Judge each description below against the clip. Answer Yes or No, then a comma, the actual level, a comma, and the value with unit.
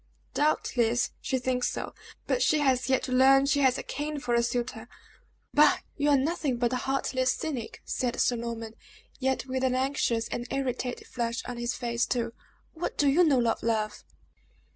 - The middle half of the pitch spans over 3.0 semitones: No, narrow, 2.4 semitones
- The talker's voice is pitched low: No, very high, 255 Hz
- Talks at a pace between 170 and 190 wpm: Yes, average, 185 wpm